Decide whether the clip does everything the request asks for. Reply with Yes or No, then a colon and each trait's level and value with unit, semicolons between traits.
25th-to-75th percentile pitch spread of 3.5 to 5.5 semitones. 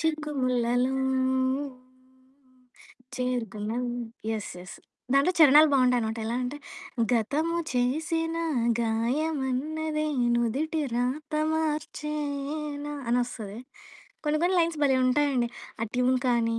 Yes: average, 3.9 semitones